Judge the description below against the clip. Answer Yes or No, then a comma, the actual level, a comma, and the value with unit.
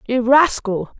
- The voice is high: Yes, high, 245 Hz